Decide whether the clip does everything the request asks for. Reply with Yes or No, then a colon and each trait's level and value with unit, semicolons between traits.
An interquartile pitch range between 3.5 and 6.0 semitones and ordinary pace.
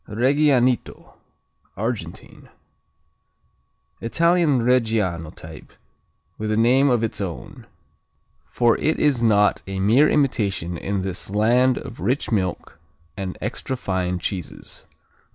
No: average, 5.0 semitones; slow, 110 wpm